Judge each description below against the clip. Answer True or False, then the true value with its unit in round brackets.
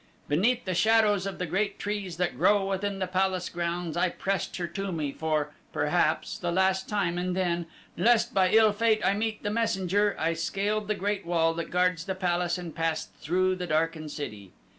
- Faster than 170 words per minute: True (195 wpm)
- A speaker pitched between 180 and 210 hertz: True (185 Hz)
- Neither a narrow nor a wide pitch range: True (3.1 semitones)